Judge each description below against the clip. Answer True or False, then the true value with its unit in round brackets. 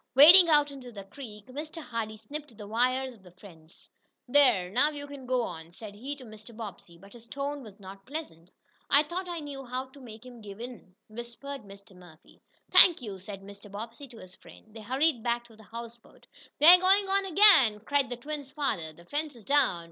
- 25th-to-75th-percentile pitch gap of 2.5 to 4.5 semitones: False (5.6 semitones)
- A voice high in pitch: True (240 Hz)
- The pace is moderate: False (210 wpm)